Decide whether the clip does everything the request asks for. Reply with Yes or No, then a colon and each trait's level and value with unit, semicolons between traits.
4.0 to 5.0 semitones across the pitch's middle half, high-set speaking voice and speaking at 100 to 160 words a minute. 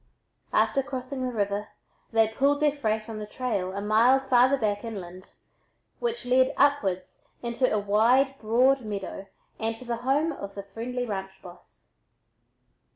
Yes: average, 4.3 semitones; high, 230 Hz; average, 155 wpm